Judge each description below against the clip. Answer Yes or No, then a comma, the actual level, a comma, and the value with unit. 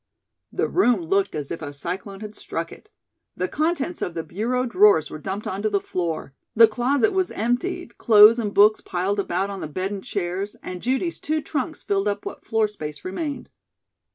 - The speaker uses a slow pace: No, average, 190 wpm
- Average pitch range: Yes, average, 5.0 semitones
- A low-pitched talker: No, high, 205 Hz